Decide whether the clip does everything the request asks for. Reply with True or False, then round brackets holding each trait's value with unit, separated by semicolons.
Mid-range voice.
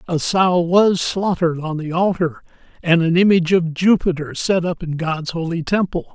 True (170 Hz)